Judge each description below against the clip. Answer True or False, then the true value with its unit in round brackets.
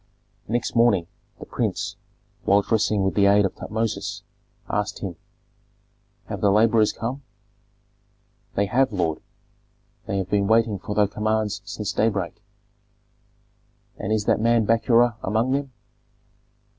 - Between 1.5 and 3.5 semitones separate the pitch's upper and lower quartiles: True (2.4 semitones)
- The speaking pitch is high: False (105 Hz)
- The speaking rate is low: True (130 wpm)